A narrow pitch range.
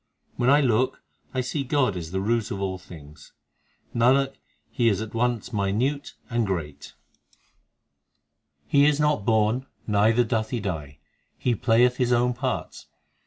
No: average, 4.2 semitones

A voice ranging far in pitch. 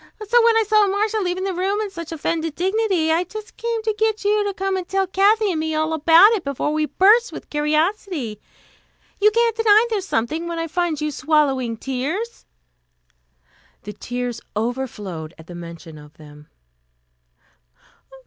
Yes: wide, 7.8 semitones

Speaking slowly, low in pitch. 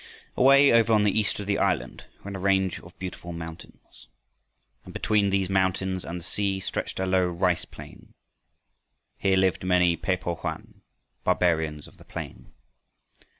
No: average, 160 wpm; very low, 95 Hz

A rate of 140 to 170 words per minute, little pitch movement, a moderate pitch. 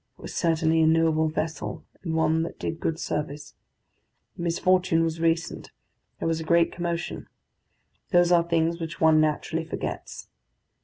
Yes: average, 155 wpm; narrow, 1.0 semitones; medium, 165 Hz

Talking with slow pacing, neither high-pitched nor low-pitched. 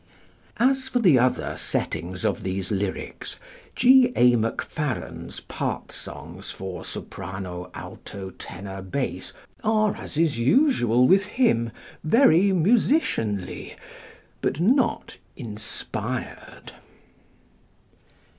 No: slow, 85 wpm; low, 125 Hz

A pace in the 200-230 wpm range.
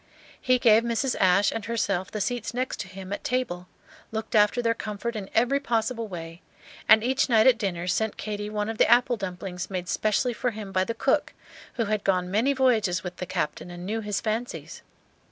Yes: fast, 205 wpm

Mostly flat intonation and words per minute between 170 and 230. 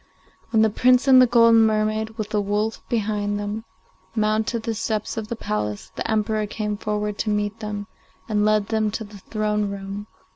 Yes: narrow, 1.1 semitones; average, 185 wpm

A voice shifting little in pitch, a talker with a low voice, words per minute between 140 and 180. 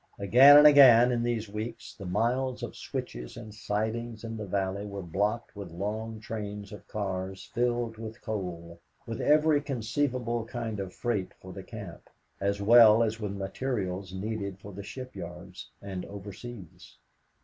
No: average, 3.3 semitones; low, 105 Hz; average, 155 wpm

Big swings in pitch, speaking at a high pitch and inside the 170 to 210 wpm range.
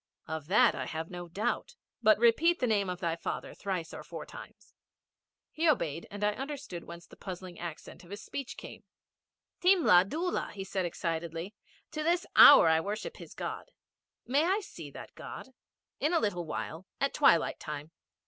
Yes: wide, 8.6 semitones; high, 195 Hz; average, 175 wpm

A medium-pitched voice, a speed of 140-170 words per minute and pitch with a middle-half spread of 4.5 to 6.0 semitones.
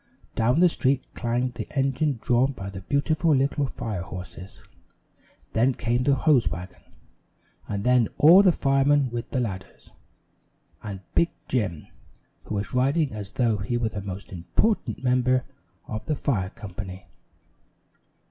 No: low, 120 Hz; average, 145 wpm; average, 5.3 semitones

